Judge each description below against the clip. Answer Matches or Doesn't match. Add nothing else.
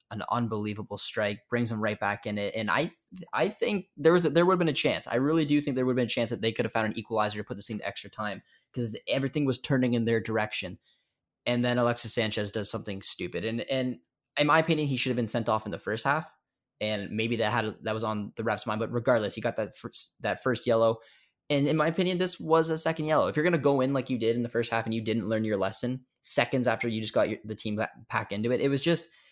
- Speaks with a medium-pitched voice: Doesn't match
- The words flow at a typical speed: Doesn't match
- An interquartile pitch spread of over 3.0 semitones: Matches